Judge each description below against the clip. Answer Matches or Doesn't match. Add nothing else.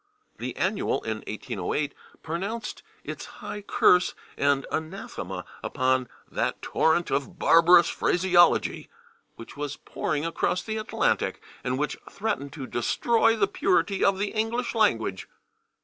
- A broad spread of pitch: Matches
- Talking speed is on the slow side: Matches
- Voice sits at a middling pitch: Matches